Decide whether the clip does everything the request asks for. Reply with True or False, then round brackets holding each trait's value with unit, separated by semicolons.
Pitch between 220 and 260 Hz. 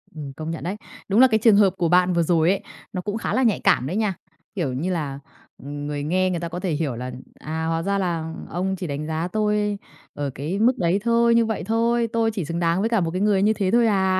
False (185 Hz)